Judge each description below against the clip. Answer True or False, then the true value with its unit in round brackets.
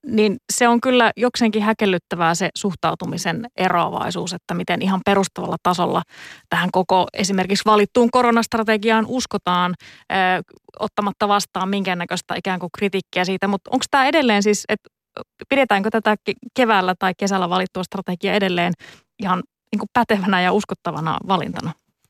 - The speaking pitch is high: True (200 Hz)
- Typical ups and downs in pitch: True (3.1 semitones)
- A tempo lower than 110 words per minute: False (135 wpm)